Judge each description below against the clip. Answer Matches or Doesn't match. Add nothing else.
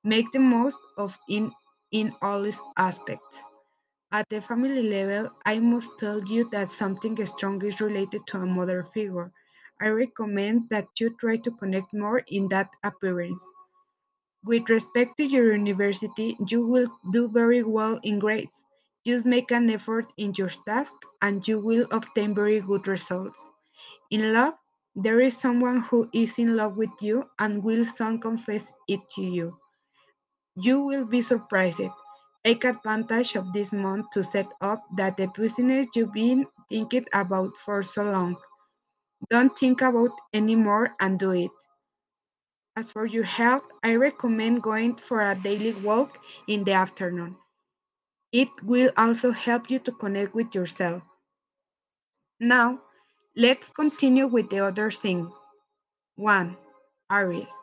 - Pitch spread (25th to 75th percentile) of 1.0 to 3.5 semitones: Matches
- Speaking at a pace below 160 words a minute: Matches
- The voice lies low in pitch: Doesn't match